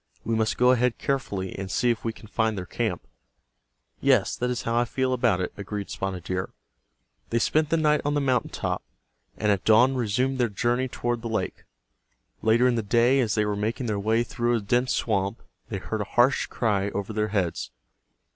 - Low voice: Yes, low, 115 Hz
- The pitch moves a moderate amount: Yes, average, 3.3 semitones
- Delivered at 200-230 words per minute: Yes, fast, 205 wpm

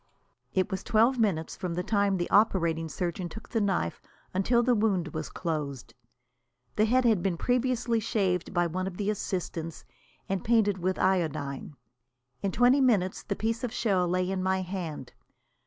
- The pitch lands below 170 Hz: No, high, 190 Hz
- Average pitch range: Yes, average, 4.2 semitones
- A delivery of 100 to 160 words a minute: No, average, 170 wpm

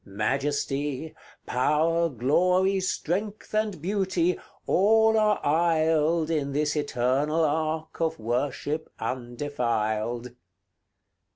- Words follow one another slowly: Yes, slow, 85 wpm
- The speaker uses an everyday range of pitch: Yes, average, 4.7 semitones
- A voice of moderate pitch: Yes, medium, 155 Hz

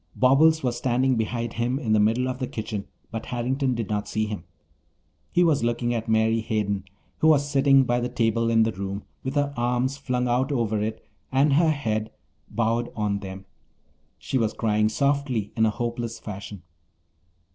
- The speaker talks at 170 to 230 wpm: Yes, average, 180 wpm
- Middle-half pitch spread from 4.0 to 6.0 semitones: No, average, 3.3 semitones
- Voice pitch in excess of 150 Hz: No, low, 120 Hz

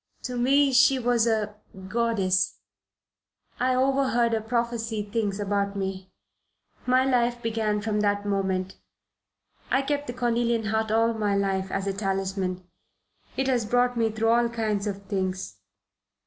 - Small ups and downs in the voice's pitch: No, average, 3.3 semitones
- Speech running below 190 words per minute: Yes, average, 145 wpm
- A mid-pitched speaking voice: No, high, 220 Hz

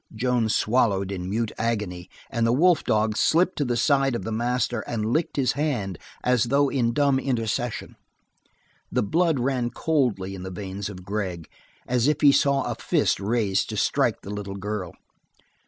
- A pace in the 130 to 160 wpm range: No, average, 175 wpm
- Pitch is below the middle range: Yes, low, 115 Hz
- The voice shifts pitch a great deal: No, average, 4.9 semitones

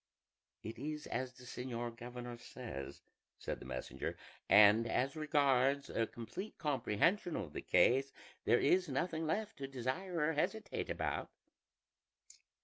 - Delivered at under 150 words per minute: Yes, slow, 135 wpm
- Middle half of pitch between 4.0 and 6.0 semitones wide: Yes, average, 4.8 semitones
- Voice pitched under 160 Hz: Yes, low, 135 Hz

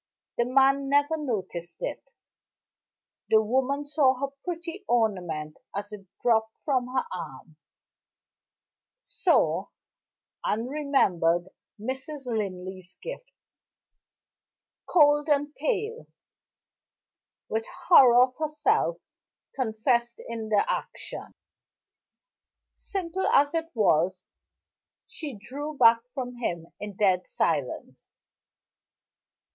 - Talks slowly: Yes, slow, 95 wpm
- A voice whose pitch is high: Yes, very high, 250 Hz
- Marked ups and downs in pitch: Yes, wide, 6.0 semitones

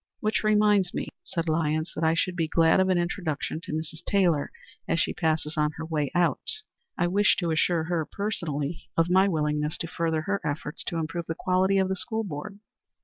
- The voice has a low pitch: No, medium, 165 Hz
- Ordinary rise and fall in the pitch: Yes, average, 3.0 semitones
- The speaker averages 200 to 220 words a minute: Yes, fast, 205 wpm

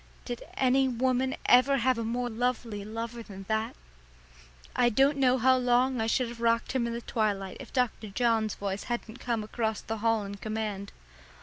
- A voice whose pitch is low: No, high, 235 Hz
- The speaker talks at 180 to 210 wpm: Yes, average, 185 wpm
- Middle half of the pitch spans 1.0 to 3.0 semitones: Yes, narrow, 2.4 semitones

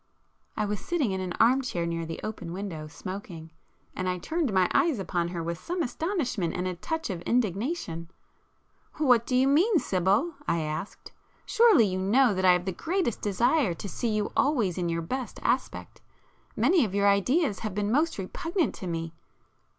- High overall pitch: Yes, high, 205 Hz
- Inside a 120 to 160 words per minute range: No, average, 180 wpm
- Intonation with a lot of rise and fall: Yes, wide, 7.1 semitones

